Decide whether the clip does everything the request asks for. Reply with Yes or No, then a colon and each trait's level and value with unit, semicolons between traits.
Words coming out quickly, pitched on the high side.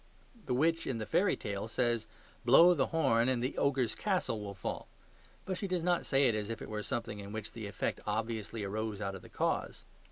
No: fast, 220 wpm; low, 115 Hz